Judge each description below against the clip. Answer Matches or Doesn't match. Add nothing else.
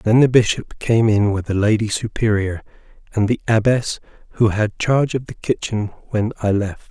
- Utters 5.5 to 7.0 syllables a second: Doesn't match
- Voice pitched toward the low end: Matches